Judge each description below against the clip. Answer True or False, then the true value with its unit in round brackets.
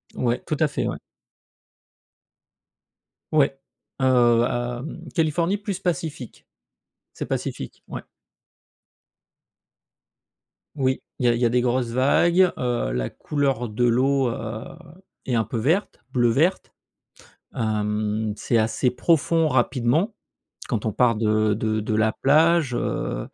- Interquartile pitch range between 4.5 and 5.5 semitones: True (5.0 semitones)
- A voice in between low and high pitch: False (125 Hz)